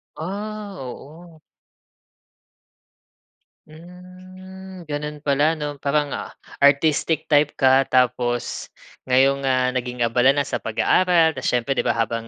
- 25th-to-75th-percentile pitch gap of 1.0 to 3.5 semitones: No, average, 4.7 semitones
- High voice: No, medium, 145 Hz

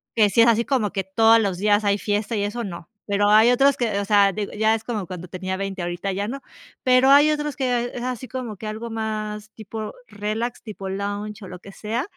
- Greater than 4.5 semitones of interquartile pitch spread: No, average, 2.8 semitones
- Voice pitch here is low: No, high, 215 Hz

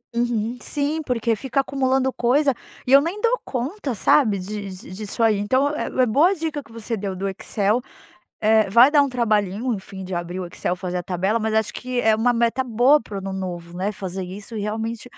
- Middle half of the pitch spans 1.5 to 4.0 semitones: No, average, 4.8 semitones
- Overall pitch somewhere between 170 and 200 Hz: No, high, 225 Hz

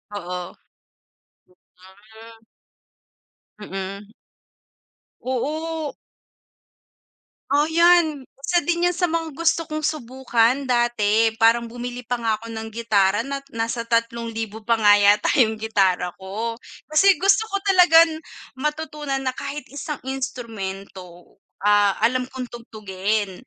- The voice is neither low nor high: No, high, 235 Hz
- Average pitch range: No, wide, 5.9 semitones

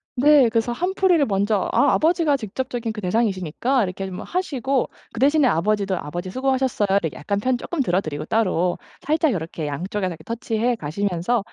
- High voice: Yes, high, 225 Hz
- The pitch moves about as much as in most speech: No, wide, 6.1 semitones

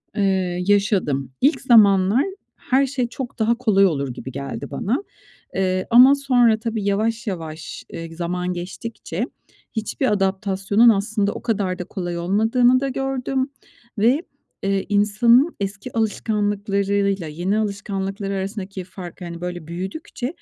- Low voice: No, high, 200 Hz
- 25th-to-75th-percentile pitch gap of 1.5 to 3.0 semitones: No, average, 3.9 semitones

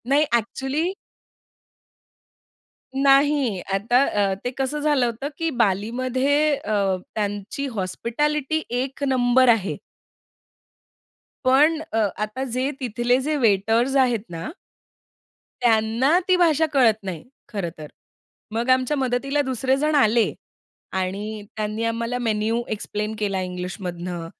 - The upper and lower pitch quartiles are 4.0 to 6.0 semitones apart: Yes, average, 4.4 semitones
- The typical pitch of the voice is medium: No, high, 240 Hz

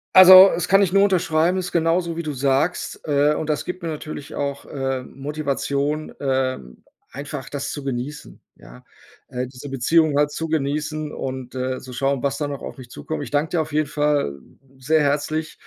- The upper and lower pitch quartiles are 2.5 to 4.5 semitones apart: Yes, average, 2.8 semitones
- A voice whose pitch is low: No, medium, 145 Hz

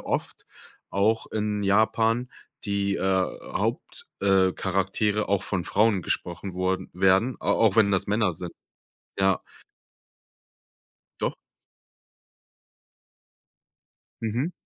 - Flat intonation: Yes, narrow, 2.3 semitones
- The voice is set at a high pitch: No, low, 100 Hz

